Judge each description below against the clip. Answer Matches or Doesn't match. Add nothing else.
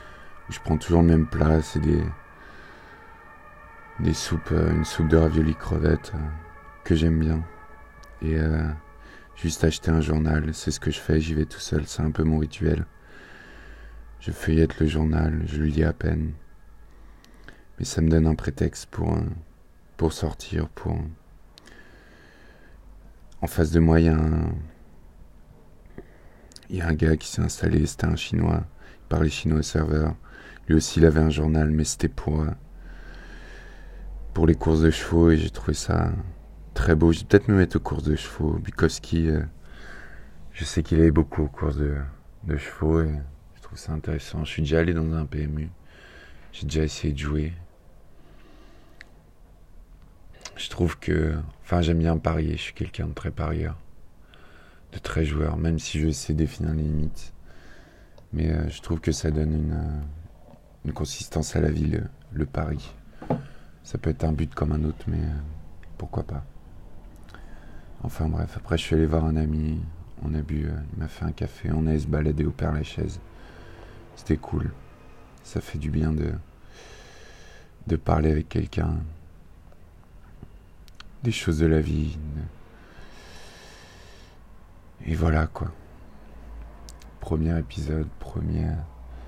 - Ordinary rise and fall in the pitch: Doesn't match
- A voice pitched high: Doesn't match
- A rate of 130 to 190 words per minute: Matches